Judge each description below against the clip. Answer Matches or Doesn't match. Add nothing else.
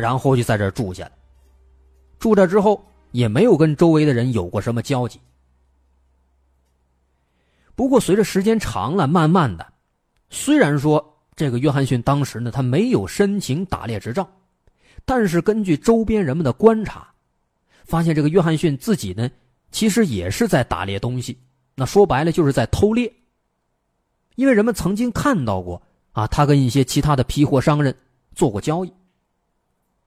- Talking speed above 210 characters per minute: Matches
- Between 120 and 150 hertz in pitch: Matches